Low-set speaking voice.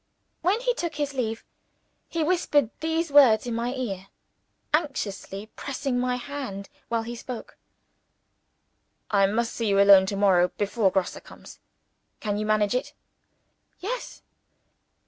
No: high, 235 Hz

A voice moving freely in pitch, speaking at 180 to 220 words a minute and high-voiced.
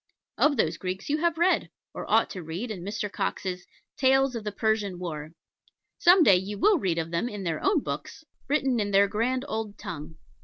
Yes: wide, 6.4 semitones; average, 200 wpm; high, 210 Hz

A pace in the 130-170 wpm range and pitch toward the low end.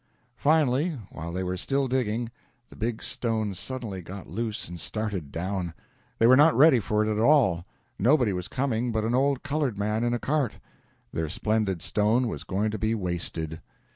No: average, 180 wpm; low, 110 Hz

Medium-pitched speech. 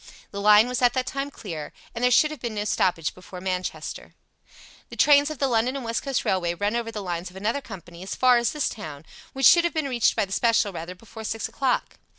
No: high, 225 Hz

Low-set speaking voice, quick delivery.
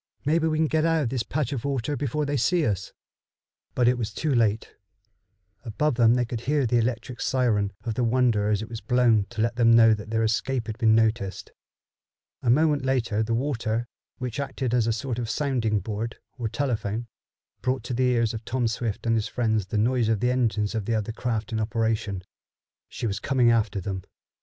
Yes: low, 115 Hz; fast, 210 wpm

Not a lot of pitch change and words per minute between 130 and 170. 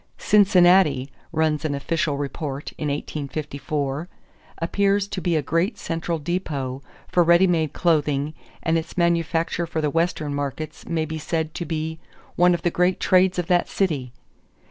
No: average, 3.0 semitones; average, 155 wpm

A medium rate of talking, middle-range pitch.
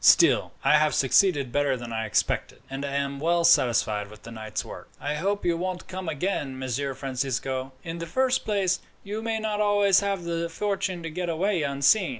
Yes: average, 195 wpm; medium, 165 Hz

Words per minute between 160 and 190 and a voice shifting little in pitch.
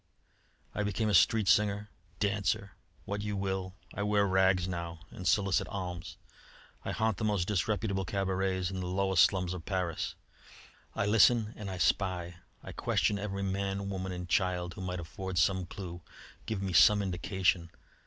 Yes: average, 165 wpm; narrow, 1.9 semitones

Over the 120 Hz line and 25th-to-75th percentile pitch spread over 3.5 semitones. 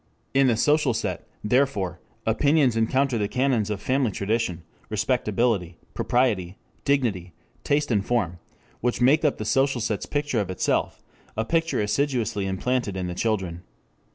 No: low, 115 Hz; average, 5.2 semitones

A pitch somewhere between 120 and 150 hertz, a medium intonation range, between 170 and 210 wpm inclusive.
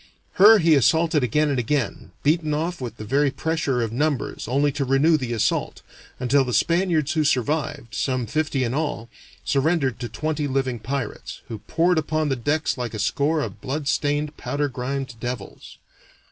Yes: medium, 140 Hz; average, 3.8 semitones; average, 175 wpm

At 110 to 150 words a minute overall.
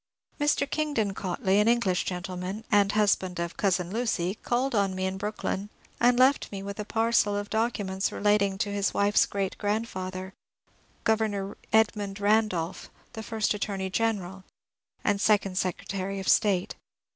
Yes: average, 145 wpm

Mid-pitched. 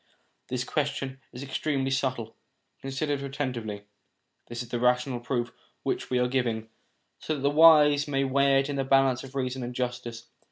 No: low, 130 Hz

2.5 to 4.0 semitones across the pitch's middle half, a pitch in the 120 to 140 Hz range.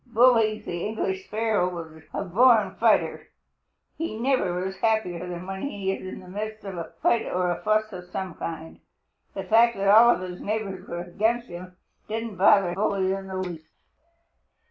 No: average, 3.3 semitones; high, 195 Hz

